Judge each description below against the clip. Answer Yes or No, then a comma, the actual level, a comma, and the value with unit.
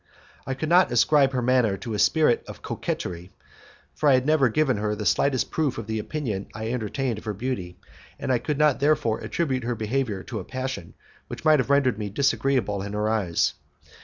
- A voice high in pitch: No, low, 125 Hz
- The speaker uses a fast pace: Yes, fast, 210 wpm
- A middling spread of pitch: Yes, average, 4.6 semitones